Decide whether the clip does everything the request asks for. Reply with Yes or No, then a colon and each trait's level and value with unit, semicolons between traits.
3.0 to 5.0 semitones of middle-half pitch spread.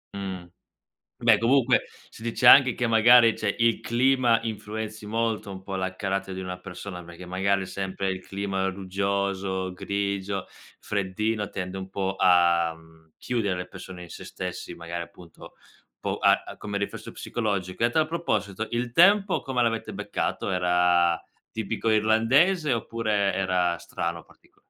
Yes: average, 3.5 semitones